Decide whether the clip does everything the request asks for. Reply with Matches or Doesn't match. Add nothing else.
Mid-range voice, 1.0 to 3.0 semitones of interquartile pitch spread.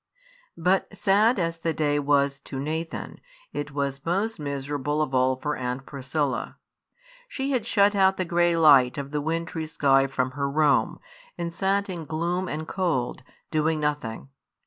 Doesn't match